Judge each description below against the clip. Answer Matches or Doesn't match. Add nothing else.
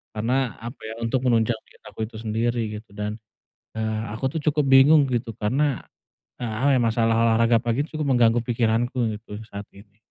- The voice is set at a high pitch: Doesn't match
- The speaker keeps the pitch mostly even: Matches